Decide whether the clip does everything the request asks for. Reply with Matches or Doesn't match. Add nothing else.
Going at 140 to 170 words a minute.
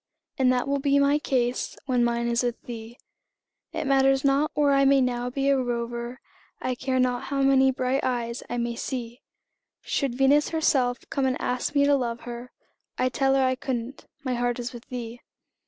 Doesn't match